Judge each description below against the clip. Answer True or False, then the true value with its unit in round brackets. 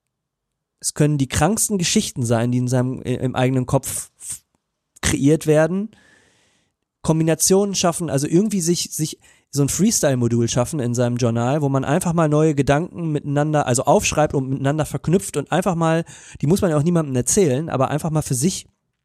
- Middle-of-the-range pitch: True (150 Hz)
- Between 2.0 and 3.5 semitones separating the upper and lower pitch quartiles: False (4.0 semitones)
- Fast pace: False (175 wpm)